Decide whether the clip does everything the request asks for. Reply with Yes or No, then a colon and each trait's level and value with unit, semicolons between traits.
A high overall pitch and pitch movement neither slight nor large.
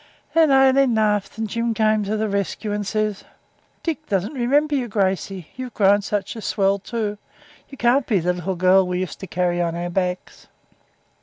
Yes: high, 210 Hz; average, 3.9 semitones